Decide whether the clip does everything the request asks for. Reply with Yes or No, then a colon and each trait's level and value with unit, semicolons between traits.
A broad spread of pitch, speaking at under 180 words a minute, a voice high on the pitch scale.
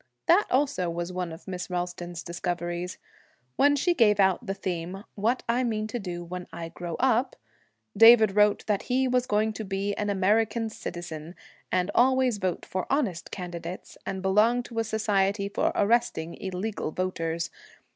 No: average, 4.2 semitones; average, 165 wpm; high, 195 Hz